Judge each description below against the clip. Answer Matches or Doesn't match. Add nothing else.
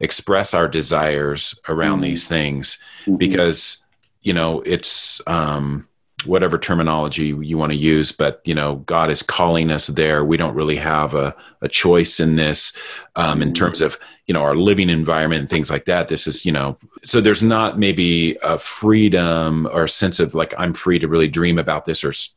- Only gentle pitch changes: Matches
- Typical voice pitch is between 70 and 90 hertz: Matches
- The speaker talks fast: Doesn't match